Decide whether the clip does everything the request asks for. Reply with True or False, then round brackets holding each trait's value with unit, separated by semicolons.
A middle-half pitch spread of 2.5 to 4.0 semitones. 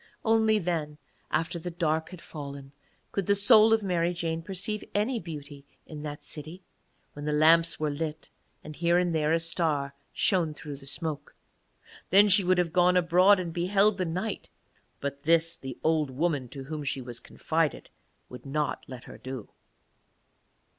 True (3.5 semitones)